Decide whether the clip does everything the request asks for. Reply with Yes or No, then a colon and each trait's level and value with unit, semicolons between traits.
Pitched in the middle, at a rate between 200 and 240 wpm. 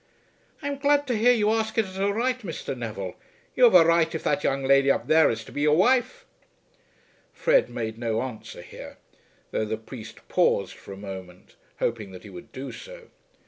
Yes: medium, 155 Hz; fast, 205 wpm